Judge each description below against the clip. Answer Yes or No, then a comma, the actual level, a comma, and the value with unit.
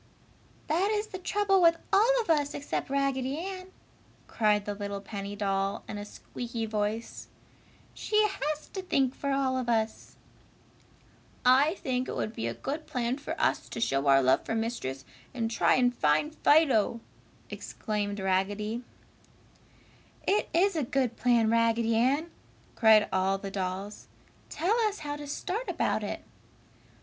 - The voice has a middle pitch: No, high, 240 Hz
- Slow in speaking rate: No, average, 155 wpm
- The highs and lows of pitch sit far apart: Yes, wide, 6.8 semitones